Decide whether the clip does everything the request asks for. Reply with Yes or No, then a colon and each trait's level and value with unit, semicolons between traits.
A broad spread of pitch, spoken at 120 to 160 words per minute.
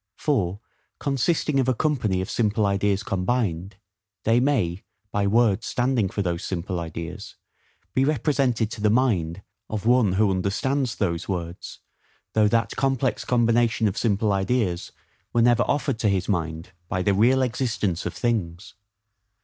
No: average, 4.7 semitones; average, 150 wpm